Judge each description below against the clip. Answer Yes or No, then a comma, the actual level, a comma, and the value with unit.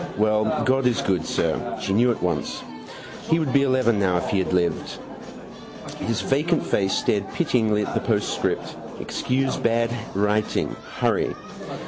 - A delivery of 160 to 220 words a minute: No, average, 150 wpm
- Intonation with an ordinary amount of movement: Yes, average, 4.6 semitones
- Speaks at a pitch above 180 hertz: No, low, 110 Hz